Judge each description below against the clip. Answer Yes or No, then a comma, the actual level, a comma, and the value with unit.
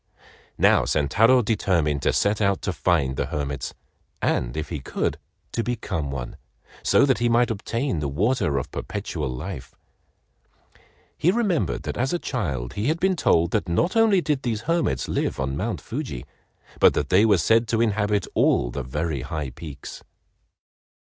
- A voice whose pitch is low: Yes, low, 100 Hz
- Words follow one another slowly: No, average, 170 wpm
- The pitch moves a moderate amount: No, wide, 8.9 semitones